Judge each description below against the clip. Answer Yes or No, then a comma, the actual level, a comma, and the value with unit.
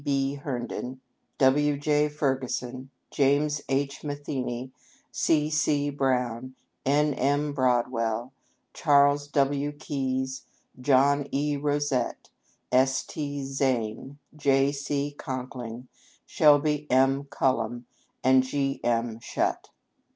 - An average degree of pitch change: No, narrow, 1.9 semitones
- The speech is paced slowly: Yes, slow, 100 wpm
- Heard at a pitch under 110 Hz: No, low, 135 Hz